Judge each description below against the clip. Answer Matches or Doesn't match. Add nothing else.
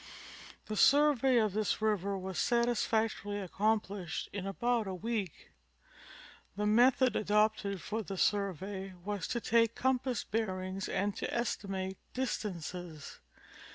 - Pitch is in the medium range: Doesn't match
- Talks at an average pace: Doesn't match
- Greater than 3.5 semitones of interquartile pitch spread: Doesn't match